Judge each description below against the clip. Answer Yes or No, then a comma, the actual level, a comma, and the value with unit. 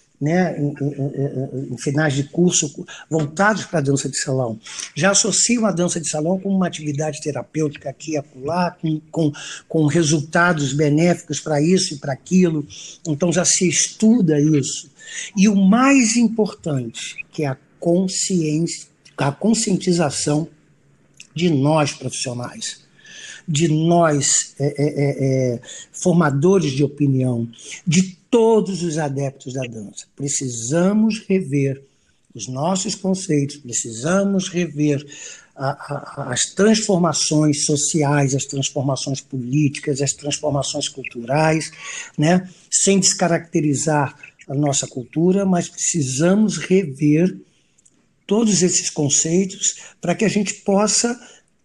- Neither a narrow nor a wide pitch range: Yes, average, 4.4 semitones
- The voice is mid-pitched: Yes, medium, 155 Hz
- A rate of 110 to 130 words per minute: Yes, slow, 120 wpm